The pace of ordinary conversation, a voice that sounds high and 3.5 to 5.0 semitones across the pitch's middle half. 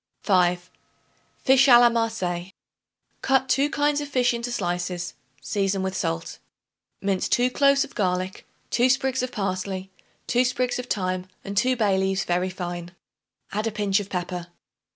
No: average, 155 wpm; high, 200 Hz; wide, 5.4 semitones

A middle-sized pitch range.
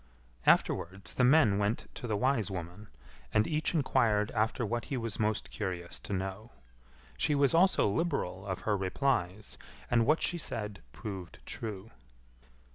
Yes: average, 4.5 semitones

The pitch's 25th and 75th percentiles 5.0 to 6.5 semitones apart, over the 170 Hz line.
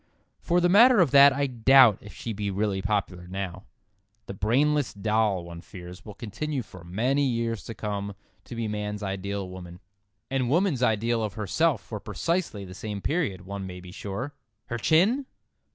No: wide, 5.5 semitones; low, 105 Hz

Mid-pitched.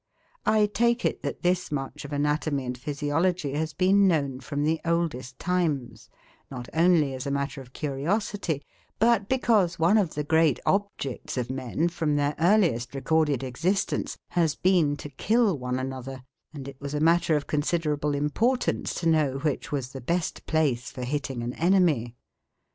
Yes: medium, 150 Hz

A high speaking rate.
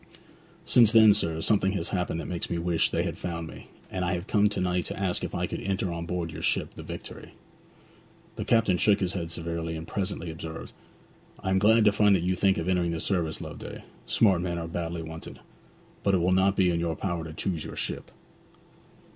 Yes: fast, 220 wpm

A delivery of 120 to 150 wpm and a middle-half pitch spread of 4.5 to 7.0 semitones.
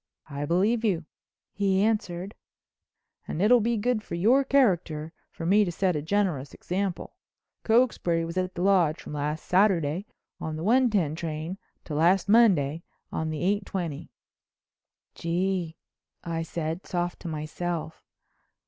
No: average, 145 wpm; average, 4.0 semitones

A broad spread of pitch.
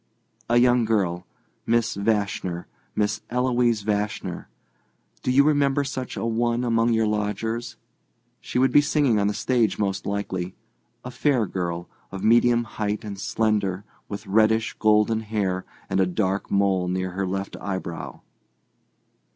No: average, 3.4 semitones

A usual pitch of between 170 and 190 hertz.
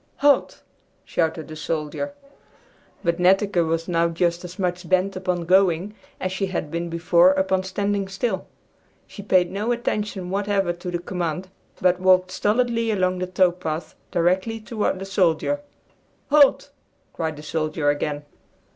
Yes: medium, 185 Hz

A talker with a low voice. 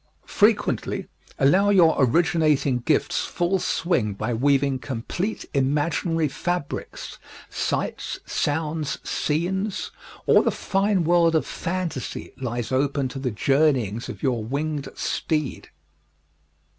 No: medium, 150 Hz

